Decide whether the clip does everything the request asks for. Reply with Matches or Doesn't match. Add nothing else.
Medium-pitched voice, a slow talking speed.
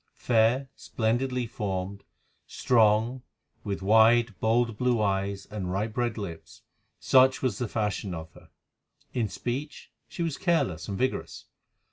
Doesn't match